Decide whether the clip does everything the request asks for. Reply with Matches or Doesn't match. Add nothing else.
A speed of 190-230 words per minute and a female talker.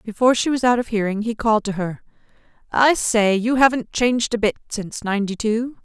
Matches